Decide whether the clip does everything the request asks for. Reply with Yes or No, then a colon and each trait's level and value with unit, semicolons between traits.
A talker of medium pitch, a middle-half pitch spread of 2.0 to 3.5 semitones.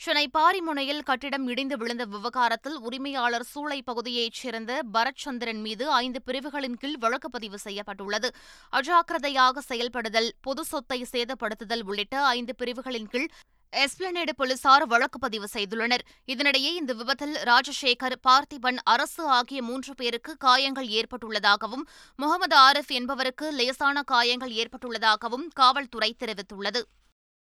No: very high, 255 Hz; average, 2.9 semitones